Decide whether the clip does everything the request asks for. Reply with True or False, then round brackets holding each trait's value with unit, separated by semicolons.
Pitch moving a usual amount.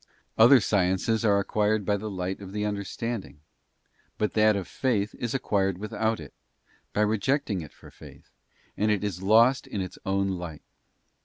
False (2.2 semitones)